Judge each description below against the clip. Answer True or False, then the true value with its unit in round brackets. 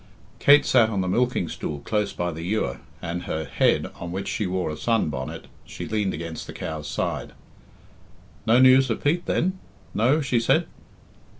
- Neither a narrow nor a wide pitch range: False (6.9 semitones)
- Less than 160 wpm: False (180 wpm)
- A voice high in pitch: False (105 Hz)